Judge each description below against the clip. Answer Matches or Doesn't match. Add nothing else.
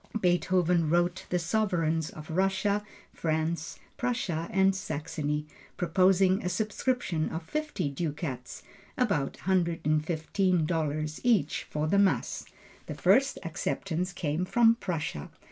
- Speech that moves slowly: Matches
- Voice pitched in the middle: Matches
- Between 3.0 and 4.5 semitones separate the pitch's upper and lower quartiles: Matches